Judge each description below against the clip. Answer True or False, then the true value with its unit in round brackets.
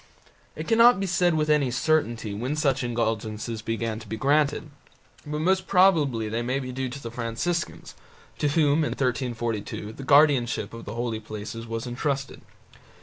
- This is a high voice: False (125 Hz)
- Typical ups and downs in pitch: True (4.7 semitones)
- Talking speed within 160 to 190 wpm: True (165 wpm)